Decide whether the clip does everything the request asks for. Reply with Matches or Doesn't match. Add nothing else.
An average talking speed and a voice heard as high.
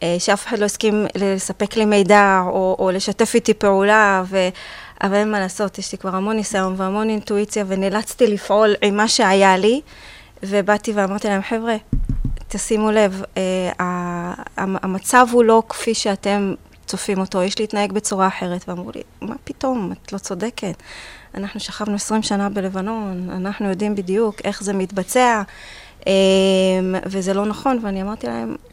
Doesn't match